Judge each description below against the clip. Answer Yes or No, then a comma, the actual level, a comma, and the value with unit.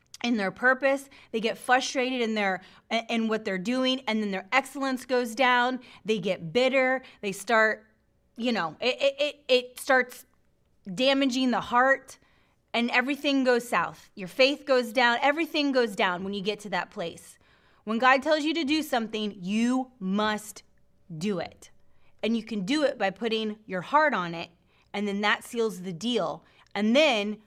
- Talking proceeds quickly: No, average, 175 wpm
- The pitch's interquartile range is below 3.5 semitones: No, average, 3.8 semitones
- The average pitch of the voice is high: Yes, high, 235 Hz